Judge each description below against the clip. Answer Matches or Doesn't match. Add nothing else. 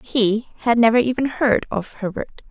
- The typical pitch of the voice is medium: Doesn't match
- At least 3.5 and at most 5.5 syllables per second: Matches